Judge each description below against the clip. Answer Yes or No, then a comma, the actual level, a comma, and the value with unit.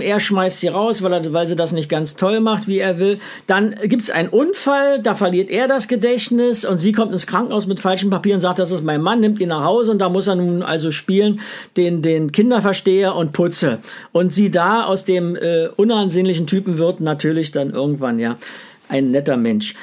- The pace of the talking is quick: Yes, fast, 220 wpm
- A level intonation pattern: No, average, 3.8 semitones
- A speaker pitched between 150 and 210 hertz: Yes, high, 190 Hz